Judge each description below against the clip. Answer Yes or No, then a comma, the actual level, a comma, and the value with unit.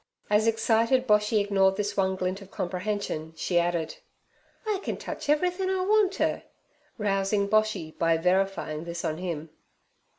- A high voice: Yes, high, 200 Hz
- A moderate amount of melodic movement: Yes, average, 4.1 semitones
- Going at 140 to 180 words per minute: Yes, average, 145 wpm